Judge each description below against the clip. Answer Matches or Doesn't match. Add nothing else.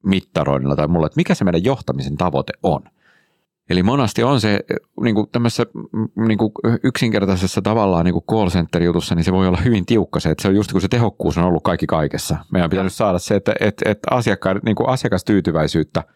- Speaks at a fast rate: Matches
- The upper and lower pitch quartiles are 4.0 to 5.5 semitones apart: Matches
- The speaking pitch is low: Matches